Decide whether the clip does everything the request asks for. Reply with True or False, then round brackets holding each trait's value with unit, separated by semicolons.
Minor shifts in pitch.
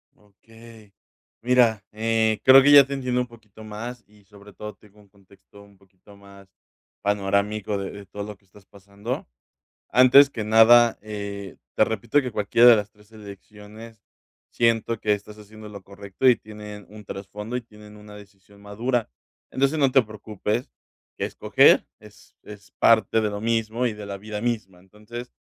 True (2.2 semitones)